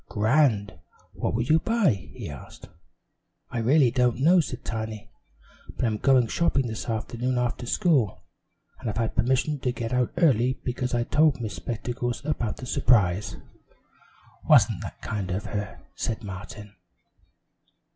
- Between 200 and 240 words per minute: No, average, 145 wpm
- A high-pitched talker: No, low, 120 Hz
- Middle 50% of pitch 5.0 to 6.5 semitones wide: No, average, 3.4 semitones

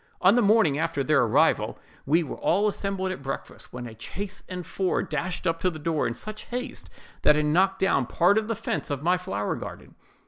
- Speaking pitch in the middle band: Yes, medium, 175 Hz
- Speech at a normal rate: No, fast, 215 wpm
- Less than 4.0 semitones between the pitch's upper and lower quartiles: No, average, 4.9 semitones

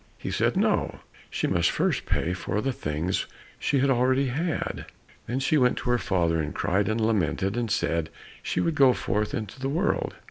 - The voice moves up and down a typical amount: No, wide, 6.3 semitones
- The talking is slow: No, average, 190 wpm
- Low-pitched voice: Yes, low, 115 Hz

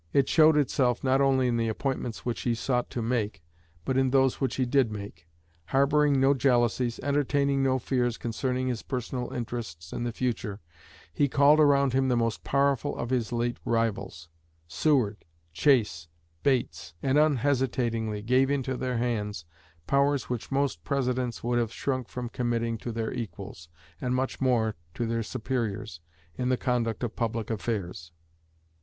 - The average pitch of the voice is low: Yes, low, 125 Hz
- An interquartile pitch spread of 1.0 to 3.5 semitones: Yes, average, 2.8 semitones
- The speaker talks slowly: No, average, 160 wpm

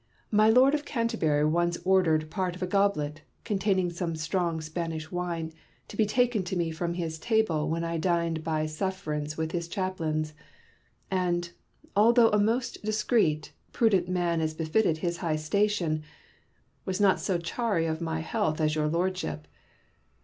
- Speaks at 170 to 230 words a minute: No, average, 155 wpm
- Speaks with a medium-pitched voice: Yes, medium, 170 Hz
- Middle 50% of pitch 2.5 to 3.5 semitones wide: No, average, 3.9 semitones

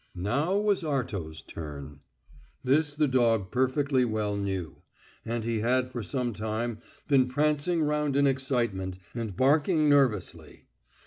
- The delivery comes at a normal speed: No, slow, 130 wpm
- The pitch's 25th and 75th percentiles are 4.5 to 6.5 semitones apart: Yes, average, 5.3 semitones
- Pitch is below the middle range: Yes, low, 125 Hz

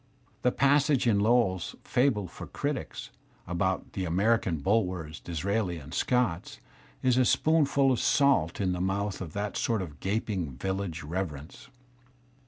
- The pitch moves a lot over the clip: Yes, wide, 5.7 semitones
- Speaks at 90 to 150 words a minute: Yes, average, 145 wpm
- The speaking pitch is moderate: No, very low, 95 Hz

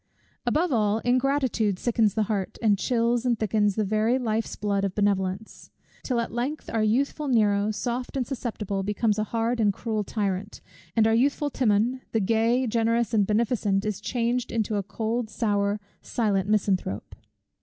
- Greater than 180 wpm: No, average, 165 wpm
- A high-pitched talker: Yes, high, 220 Hz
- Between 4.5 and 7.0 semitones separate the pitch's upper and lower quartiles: No, narrow, 2.6 semitones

